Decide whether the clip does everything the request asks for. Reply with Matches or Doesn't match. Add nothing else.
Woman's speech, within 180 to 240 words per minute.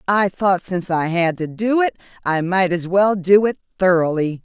Matches